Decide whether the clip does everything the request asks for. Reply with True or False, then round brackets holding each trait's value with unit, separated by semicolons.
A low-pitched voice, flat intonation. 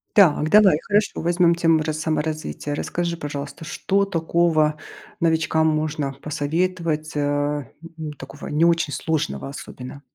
False (155 Hz; 2.3 semitones)